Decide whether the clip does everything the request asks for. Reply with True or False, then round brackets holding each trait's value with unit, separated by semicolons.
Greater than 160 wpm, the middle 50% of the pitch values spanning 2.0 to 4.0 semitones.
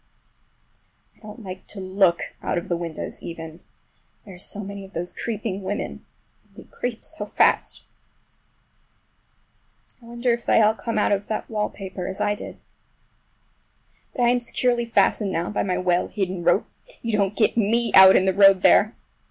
True (170 wpm; 3.3 semitones)